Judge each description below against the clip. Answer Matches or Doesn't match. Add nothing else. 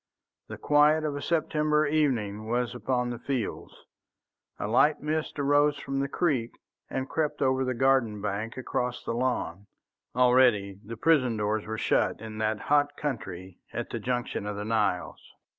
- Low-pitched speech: Matches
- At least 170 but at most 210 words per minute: Doesn't match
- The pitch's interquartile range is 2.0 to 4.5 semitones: Doesn't match